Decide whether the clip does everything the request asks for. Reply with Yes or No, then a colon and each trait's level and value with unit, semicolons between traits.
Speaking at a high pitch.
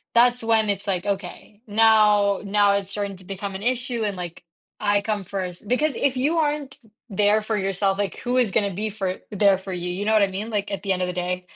Yes: high, 205 Hz